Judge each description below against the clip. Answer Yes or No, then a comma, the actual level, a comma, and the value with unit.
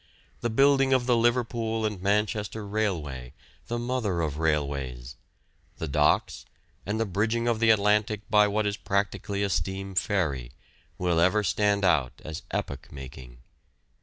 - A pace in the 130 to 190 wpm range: Yes, average, 145 wpm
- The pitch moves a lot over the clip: Yes, wide, 6.1 semitones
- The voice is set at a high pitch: No, low, 100 Hz